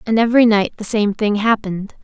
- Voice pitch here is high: Yes, high, 215 Hz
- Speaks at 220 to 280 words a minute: No, fast, 205 wpm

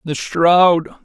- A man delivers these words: Yes, male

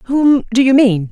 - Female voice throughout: Yes, female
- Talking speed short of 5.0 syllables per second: Yes, 4.1 syllables/s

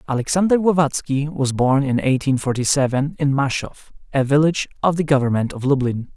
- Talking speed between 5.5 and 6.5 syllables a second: Yes, 5.8 syllables/s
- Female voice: No, male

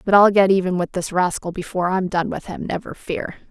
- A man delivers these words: No, female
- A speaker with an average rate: No, fast, 240 wpm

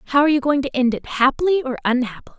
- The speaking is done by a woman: Yes, female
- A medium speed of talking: No, fast, 225 wpm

